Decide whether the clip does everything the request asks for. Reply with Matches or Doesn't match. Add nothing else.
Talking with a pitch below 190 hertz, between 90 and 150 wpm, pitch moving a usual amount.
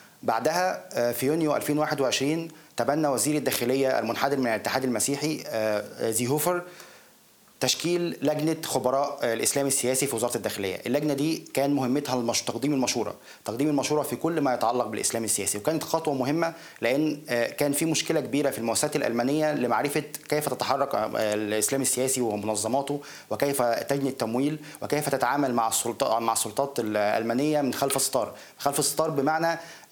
Matches